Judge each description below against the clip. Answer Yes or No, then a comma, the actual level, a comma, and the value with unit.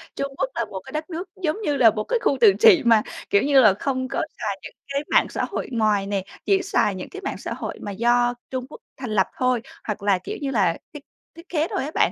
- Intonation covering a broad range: Yes, wide, 6.4 semitones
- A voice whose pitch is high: Yes, very high, 255 Hz